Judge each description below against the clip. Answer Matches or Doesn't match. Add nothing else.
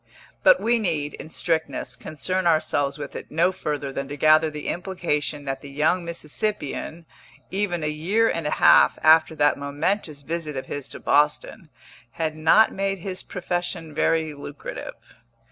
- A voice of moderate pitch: Matches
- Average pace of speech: Matches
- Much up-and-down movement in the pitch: Doesn't match